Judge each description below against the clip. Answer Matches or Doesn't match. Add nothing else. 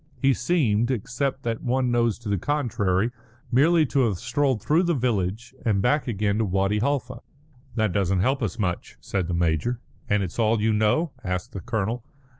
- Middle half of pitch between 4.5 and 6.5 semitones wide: Matches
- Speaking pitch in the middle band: Doesn't match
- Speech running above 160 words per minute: Matches